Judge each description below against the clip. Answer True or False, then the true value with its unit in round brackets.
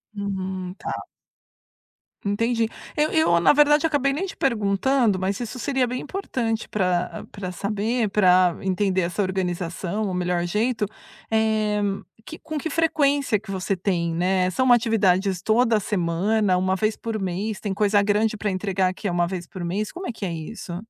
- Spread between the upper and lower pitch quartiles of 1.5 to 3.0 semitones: False (3.7 semitones)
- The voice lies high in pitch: True (205 Hz)